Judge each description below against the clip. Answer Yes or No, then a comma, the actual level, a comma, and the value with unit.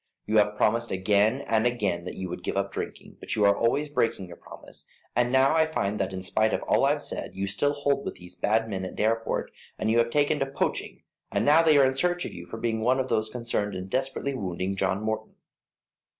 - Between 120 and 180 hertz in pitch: No, low, 110 Hz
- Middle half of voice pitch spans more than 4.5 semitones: Yes, average, 5.1 semitones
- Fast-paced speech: Yes, fast, 240 wpm